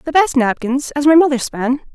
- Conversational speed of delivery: No, fast, 215 wpm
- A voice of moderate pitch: No, very high, 275 Hz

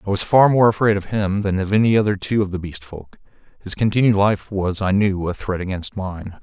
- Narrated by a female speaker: No, male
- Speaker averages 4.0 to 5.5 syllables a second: Yes, 5.4 syllables/s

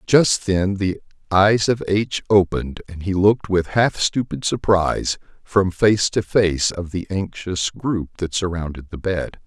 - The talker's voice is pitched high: No, very low, 95 Hz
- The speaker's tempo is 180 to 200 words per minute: No, average, 165 wpm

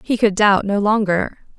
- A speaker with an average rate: Yes, average, 190 wpm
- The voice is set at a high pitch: Yes, high, 205 Hz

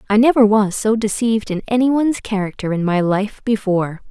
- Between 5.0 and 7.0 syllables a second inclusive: Yes, 5.5 syllables/s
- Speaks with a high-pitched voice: Yes, high, 215 Hz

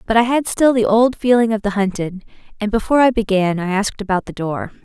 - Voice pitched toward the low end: No, high, 215 Hz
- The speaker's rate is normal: No, fast, 235 wpm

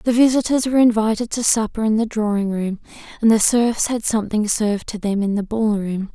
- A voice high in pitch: Yes, high, 220 Hz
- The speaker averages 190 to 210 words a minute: Yes, fast, 205 wpm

